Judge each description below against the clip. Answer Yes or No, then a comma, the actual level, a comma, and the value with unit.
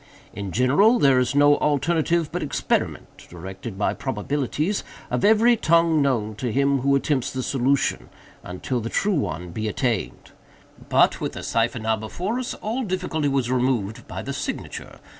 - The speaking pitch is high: No, low, 135 Hz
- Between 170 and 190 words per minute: No, average, 160 wpm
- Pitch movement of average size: No, wide, 6.2 semitones